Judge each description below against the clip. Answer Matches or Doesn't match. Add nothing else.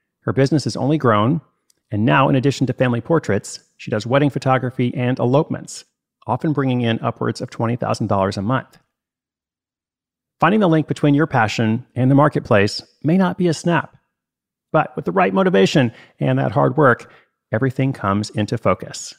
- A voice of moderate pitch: Doesn't match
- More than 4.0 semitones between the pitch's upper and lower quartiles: Matches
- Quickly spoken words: Doesn't match